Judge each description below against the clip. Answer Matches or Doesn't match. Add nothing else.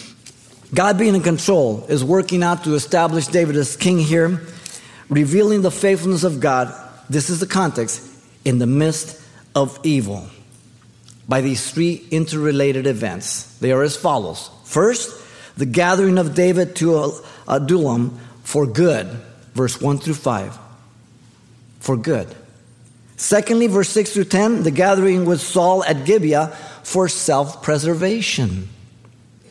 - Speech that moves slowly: Matches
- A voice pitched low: Doesn't match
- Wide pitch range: Matches